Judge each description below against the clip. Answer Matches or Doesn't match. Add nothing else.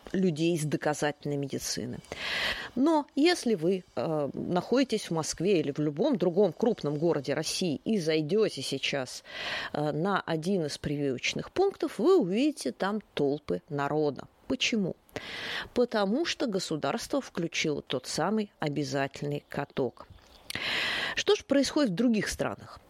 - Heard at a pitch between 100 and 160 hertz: Doesn't match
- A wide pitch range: Matches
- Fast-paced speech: Doesn't match